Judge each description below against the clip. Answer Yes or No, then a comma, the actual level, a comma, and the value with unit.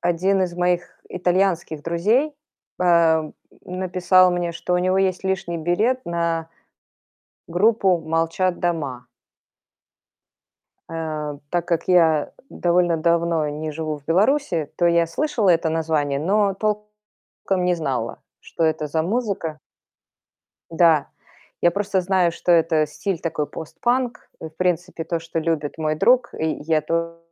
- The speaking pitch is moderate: Yes, medium, 170 Hz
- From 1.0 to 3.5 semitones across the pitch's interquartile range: Yes, narrow, 2.5 semitones